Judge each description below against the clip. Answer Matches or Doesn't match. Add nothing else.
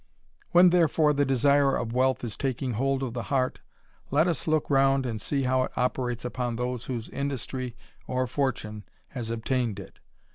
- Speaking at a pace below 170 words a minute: Doesn't match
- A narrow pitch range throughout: Matches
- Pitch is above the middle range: Doesn't match